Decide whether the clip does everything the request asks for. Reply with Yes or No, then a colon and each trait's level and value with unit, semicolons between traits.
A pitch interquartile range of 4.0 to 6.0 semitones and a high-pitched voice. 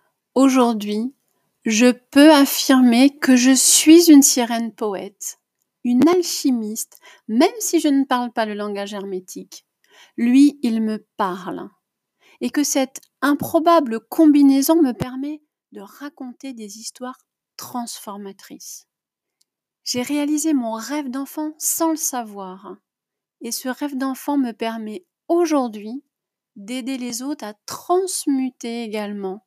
Yes: average, 4.4 semitones; very high, 260 Hz